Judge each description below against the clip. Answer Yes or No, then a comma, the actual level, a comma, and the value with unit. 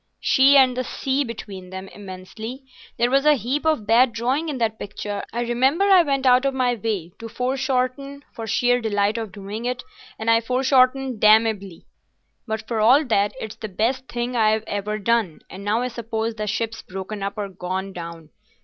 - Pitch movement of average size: Yes, average, 3.7 semitones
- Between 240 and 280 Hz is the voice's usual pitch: No, high, 230 Hz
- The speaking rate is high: No, average, 185 wpm